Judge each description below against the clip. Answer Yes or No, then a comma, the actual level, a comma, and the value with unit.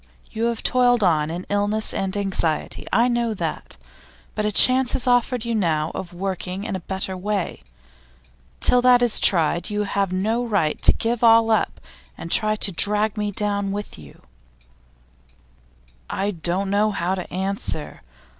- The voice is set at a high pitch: Yes, high, 205 Hz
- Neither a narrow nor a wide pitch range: Yes, average, 3.4 semitones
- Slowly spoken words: No, average, 165 wpm